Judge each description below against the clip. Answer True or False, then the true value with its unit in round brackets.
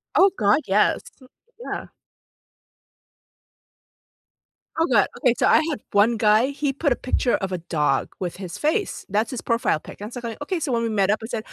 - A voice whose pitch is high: True (230 Hz)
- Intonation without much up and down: False (5.0 semitones)